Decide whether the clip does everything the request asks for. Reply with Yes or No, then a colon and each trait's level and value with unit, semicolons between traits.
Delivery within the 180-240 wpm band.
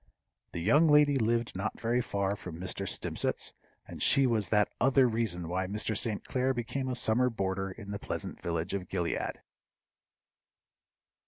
No: average, 160 wpm